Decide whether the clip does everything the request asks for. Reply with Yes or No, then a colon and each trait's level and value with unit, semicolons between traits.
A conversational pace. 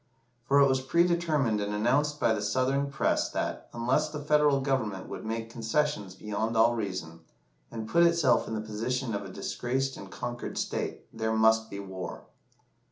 Yes: average, 170 wpm